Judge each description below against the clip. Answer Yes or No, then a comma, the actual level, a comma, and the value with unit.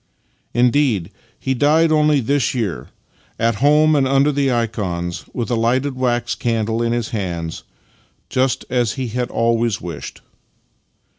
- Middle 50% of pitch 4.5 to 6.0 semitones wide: No, average, 3.2 semitones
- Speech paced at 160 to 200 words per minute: No, average, 145 wpm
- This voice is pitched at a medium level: No, low, 120 Hz